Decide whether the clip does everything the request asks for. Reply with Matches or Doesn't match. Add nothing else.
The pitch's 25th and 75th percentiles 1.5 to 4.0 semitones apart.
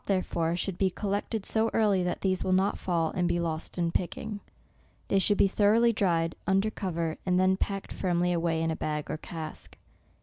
Matches